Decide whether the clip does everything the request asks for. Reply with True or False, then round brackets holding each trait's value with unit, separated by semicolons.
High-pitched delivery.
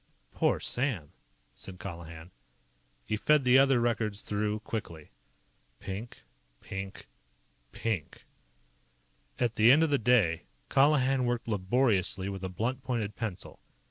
False (110 Hz)